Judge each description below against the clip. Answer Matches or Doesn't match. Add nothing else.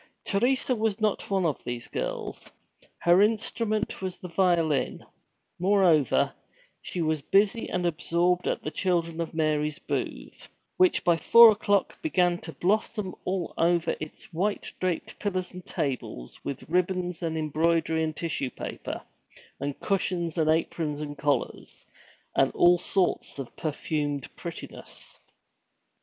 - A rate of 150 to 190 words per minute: Doesn't match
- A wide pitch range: Doesn't match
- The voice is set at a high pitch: Doesn't match